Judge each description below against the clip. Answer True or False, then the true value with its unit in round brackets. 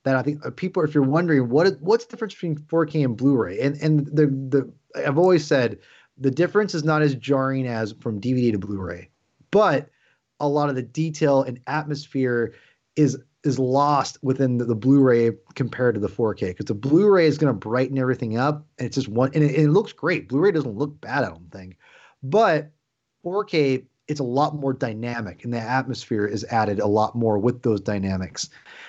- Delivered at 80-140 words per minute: False (200 wpm)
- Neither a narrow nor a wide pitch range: True (4.0 semitones)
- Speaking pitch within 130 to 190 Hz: True (135 Hz)